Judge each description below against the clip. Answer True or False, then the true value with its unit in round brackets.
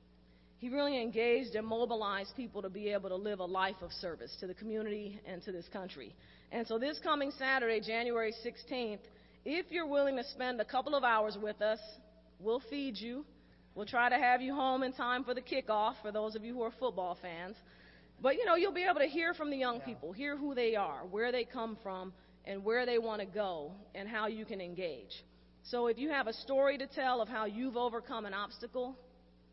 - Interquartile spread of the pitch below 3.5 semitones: False (3.8 semitones)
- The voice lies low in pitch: False (230 Hz)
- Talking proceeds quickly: True (215 wpm)